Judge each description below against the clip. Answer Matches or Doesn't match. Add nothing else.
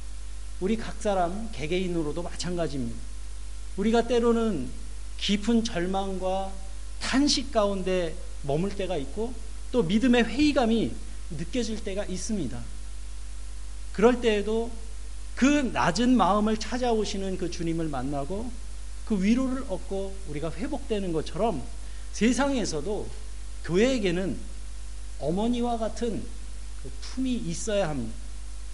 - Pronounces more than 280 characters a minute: Doesn't match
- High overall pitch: Matches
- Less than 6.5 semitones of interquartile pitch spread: Doesn't match